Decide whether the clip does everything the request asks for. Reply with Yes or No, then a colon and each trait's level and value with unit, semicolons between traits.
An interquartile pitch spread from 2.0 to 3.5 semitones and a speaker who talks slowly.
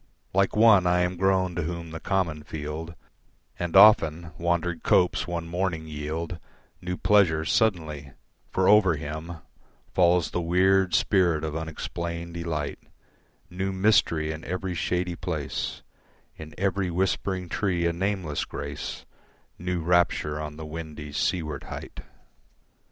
Yes: narrow, 2.6 semitones; slow, 130 wpm